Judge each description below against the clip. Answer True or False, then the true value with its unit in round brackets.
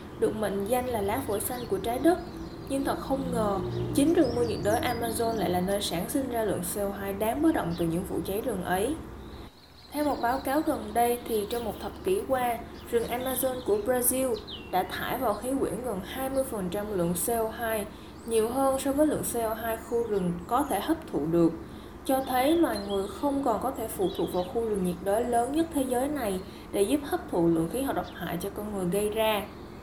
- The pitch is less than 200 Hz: False (230 Hz)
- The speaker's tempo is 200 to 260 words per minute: True (220 wpm)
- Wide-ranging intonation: False (5.0 semitones)